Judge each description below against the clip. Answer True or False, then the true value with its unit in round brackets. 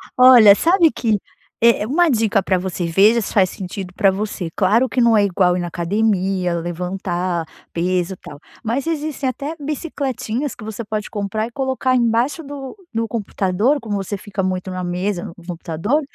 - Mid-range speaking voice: False (210 Hz)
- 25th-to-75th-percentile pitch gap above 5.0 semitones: True (5.4 semitones)